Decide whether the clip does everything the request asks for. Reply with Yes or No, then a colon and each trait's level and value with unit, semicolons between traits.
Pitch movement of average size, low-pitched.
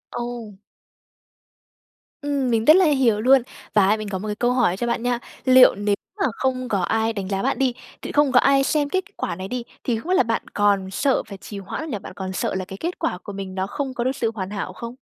No: average, 4.8 semitones; high, 230 Hz